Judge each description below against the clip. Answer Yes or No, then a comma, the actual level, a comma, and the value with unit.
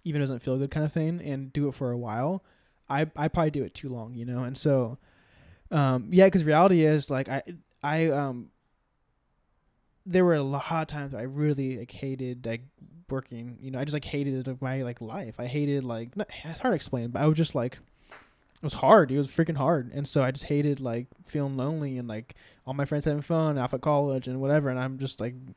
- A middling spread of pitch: Yes, average, 3.2 semitones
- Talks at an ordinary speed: No, fast, 235 wpm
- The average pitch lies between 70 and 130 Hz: No, medium, 140 Hz